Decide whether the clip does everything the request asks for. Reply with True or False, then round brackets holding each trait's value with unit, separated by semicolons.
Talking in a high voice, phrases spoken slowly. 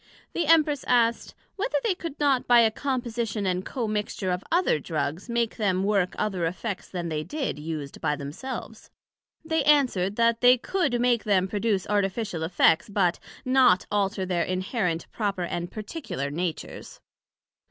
False (210 Hz; 150 wpm)